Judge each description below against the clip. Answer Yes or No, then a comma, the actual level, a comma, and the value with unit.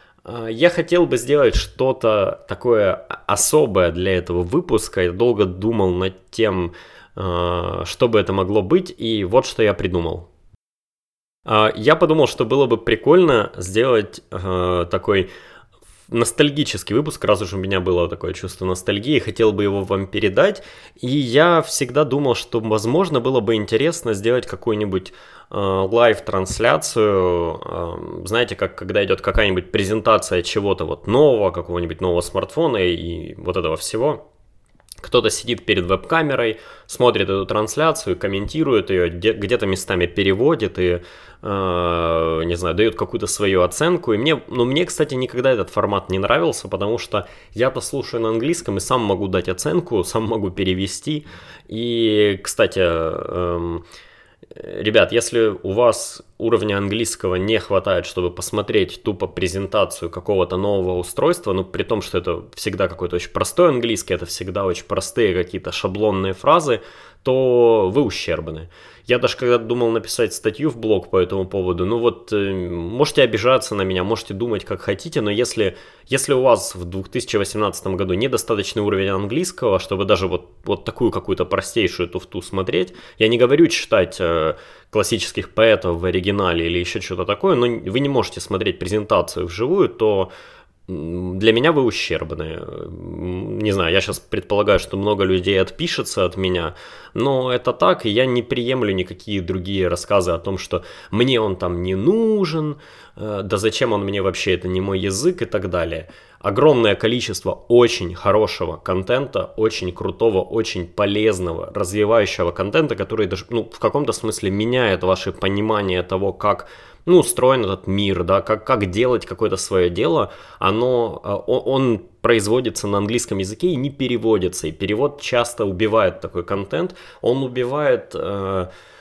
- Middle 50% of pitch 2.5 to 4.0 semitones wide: No, average, 4.4 semitones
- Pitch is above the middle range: No, low, 100 Hz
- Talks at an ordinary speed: Yes, average, 150 wpm